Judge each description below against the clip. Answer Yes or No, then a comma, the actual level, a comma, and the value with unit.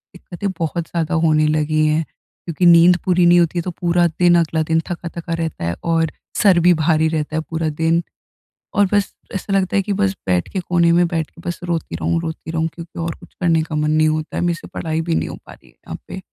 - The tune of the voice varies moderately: No, narrow, 1.9 semitones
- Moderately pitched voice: Yes, medium, 165 Hz